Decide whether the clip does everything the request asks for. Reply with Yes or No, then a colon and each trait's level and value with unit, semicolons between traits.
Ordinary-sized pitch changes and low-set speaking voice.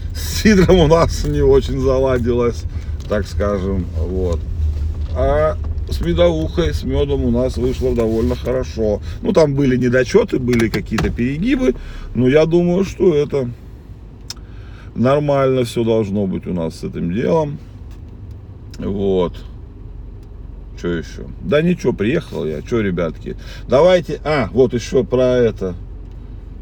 No: wide, 6.6 semitones; low, 110 Hz